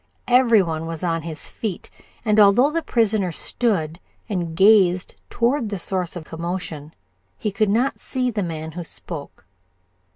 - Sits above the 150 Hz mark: Yes, high, 190 Hz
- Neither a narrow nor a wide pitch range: Yes, average, 5.0 semitones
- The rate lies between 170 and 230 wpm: No, average, 155 wpm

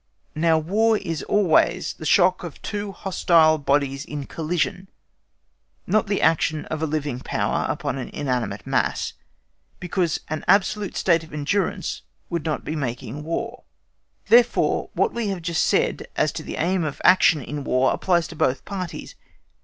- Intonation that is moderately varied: Yes, average, 4.1 semitones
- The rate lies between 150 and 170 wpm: Yes, average, 160 wpm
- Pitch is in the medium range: Yes, medium, 165 Hz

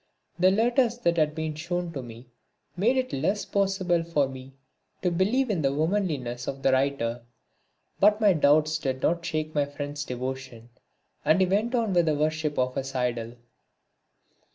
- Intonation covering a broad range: Yes, wide, 5.9 semitones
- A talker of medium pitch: Yes, medium, 155 Hz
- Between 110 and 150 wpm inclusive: No, average, 170 wpm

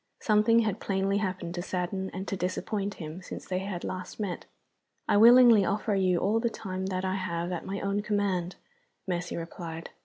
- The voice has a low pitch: No, high, 190 Hz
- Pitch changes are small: Yes, narrow, 2.2 semitones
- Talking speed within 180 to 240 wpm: Yes, average, 185 wpm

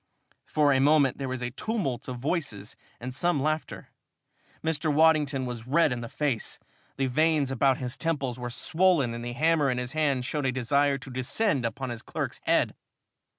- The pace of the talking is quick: No, average, 185 wpm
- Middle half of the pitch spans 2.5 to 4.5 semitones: Yes, average, 3.8 semitones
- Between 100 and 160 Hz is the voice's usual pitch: Yes, low, 135 Hz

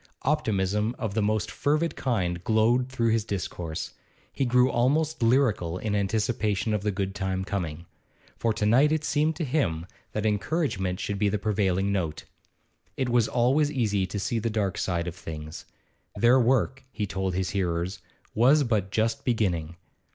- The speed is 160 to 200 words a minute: Yes, average, 170 wpm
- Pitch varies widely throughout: No, average, 4.5 semitones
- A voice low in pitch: Yes, low, 105 Hz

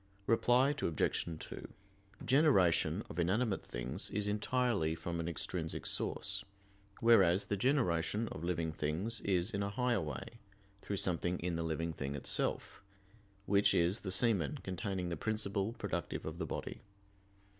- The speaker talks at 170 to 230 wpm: No, average, 145 wpm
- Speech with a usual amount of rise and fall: Yes, average, 4.9 semitones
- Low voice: Yes, very low, 95 Hz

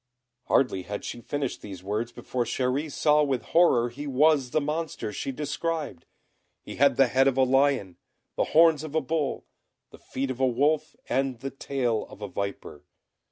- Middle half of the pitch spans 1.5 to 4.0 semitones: Yes, average, 3.7 semitones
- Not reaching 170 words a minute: No, average, 180 wpm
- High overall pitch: No, low, 135 Hz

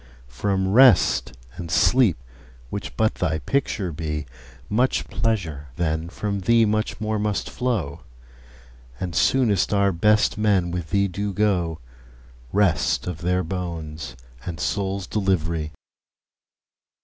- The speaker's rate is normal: No, slow, 125 wpm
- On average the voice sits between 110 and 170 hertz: No, very low, 95 Hz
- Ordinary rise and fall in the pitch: Yes, average, 4.1 semitones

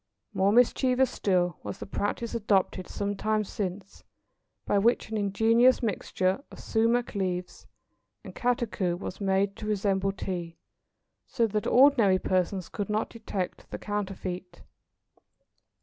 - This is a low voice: No, high, 200 Hz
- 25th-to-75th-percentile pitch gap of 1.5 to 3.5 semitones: Yes, average, 3.1 semitones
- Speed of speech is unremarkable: No, slow, 130 wpm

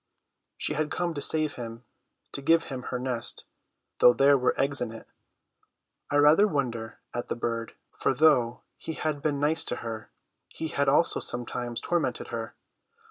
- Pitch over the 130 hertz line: Yes, medium, 140 Hz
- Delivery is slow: No, average, 170 wpm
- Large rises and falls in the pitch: No, average, 4.2 semitones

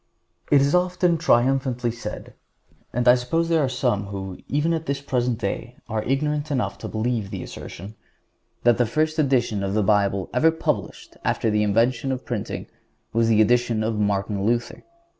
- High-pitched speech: No, low, 120 Hz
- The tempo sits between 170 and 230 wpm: Yes, average, 175 wpm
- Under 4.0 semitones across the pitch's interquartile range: No, average, 4.3 semitones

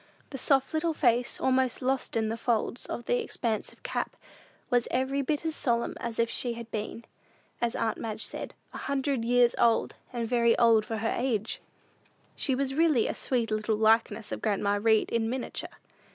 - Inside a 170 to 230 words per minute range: Yes, average, 180 wpm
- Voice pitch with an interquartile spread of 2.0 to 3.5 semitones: Yes, average, 2.7 semitones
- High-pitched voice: Yes, high, 235 Hz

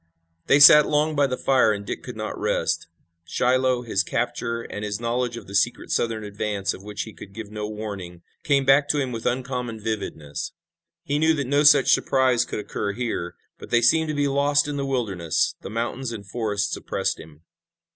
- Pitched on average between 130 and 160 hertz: No, low, 120 Hz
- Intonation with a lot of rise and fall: No, average, 4.8 semitones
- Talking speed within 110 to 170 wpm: No, average, 200 wpm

